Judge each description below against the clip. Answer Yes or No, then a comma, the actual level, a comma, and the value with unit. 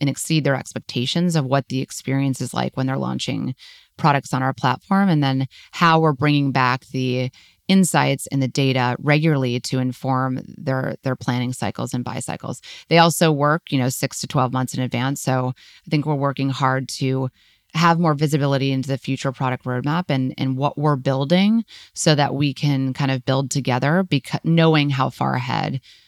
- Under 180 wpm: No, average, 190 wpm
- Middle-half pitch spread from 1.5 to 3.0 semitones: Yes, narrow, 2.5 semitones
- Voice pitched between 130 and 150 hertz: Yes, low, 135 Hz